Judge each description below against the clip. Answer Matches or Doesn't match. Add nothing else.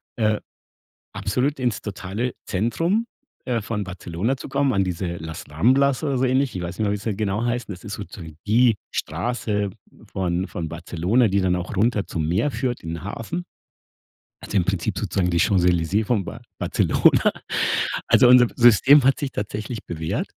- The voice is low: Matches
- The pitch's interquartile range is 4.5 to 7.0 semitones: Matches